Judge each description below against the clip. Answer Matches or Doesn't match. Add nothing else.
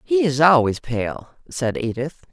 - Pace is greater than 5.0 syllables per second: Doesn't match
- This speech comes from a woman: Matches